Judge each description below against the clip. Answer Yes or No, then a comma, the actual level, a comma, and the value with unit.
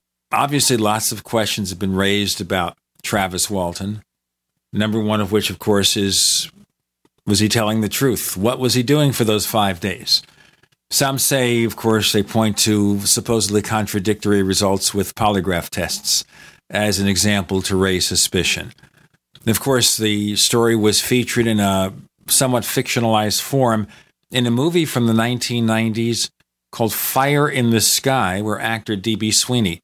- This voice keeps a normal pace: Yes, average, 150 wpm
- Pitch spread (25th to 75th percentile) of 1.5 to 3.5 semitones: Yes, average, 2.9 semitones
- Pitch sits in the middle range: No, low, 105 Hz